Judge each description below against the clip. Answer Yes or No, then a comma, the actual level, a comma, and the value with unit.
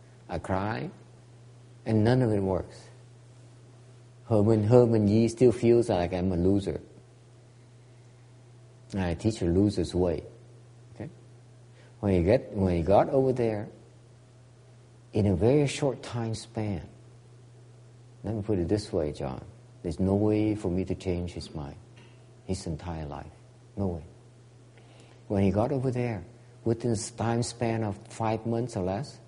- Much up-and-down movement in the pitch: No, average, 3.0 semitones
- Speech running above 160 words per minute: No, average, 150 wpm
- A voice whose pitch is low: Yes, low, 120 Hz